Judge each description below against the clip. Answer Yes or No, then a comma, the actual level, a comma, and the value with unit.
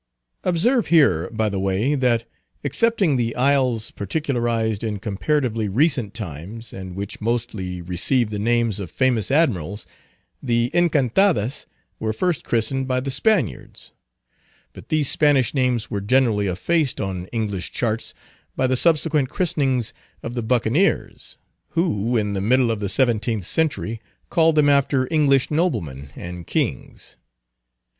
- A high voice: No, low, 120 Hz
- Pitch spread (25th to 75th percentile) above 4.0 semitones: Yes, average, 5.3 semitones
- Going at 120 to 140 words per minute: Yes, slow, 135 wpm